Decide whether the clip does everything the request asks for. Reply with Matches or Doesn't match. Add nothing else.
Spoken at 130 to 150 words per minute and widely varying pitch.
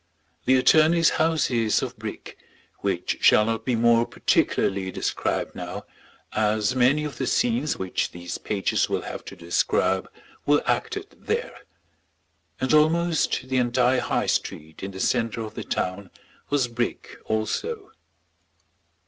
Matches